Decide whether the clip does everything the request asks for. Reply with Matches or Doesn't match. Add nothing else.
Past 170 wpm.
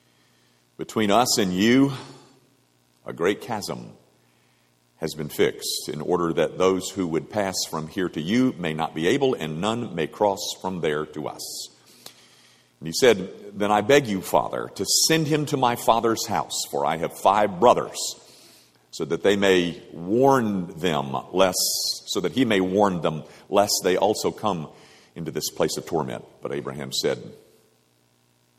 Doesn't match